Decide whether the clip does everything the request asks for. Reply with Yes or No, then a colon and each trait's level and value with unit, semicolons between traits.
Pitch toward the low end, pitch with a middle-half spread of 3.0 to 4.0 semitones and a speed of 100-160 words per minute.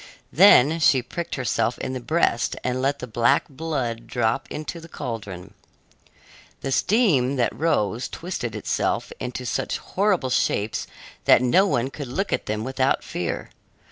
No: low, 130 Hz; average, 5.2 semitones; average, 150 wpm